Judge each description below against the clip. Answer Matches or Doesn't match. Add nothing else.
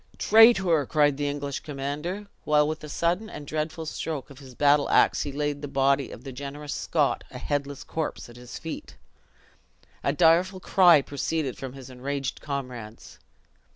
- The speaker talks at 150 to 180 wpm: Matches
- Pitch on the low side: Doesn't match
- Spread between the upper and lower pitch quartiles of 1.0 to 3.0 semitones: Matches